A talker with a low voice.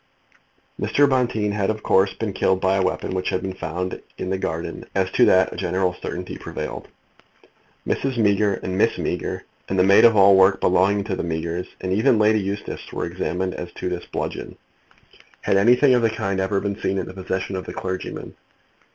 Yes: very low, 95 Hz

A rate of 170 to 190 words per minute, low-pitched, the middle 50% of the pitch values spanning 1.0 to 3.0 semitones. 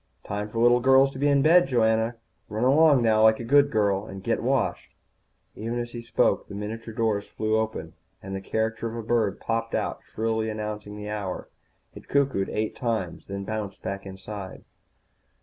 Yes: average, 185 wpm; low, 110 Hz; narrow, 2.4 semitones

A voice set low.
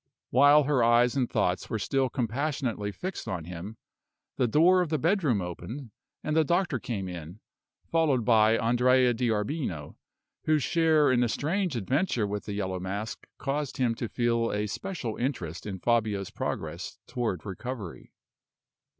Yes: low, 120 Hz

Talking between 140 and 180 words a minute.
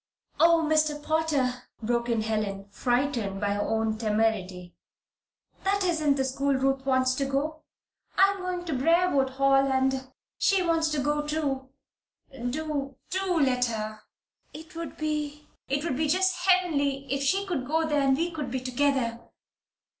Yes: average, 160 wpm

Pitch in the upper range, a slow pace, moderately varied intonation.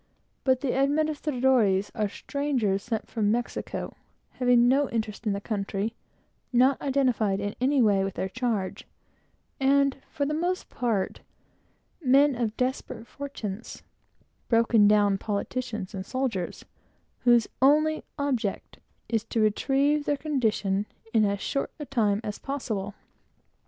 Yes: high, 240 Hz; slow, 130 wpm; average, 4.9 semitones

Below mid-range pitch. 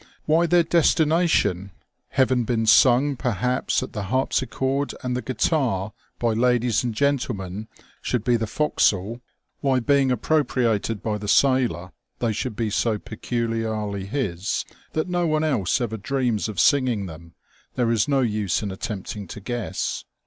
Yes: low, 120 Hz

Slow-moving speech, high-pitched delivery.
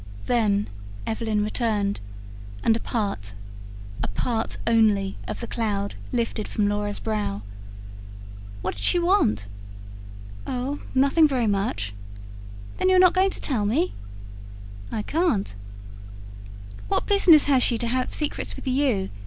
Yes: slow, 130 wpm; high, 225 Hz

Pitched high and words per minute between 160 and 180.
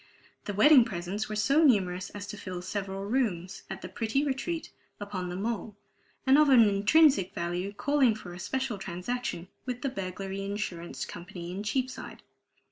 Yes: high, 205 Hz; average, 165 wpm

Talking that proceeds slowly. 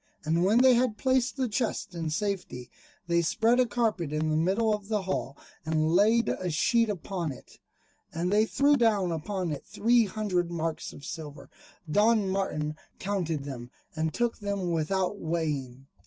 No: average, 170 wpm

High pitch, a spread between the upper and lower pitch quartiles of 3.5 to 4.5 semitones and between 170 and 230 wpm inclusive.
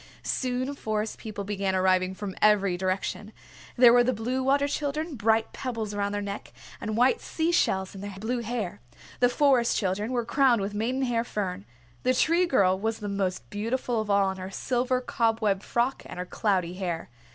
Yes: high, 220 Hz; average, 4.2 semitones; average, 185 wpm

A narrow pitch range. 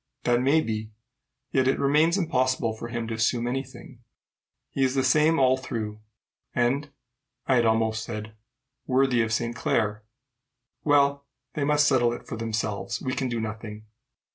No: average, 3.4 semitones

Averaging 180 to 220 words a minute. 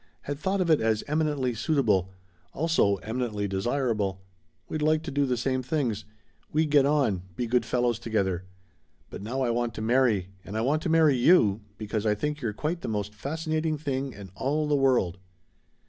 Yes: average, 185 wpm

